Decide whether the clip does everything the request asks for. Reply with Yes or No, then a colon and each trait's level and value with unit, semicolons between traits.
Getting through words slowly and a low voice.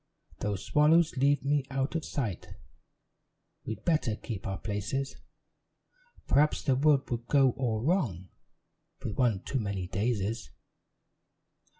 Yes: slow, 120 wpm; low, 125 Hz